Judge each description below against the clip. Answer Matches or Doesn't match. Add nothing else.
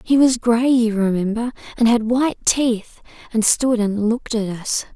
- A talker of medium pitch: Doesn't match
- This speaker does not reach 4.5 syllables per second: Doesn't match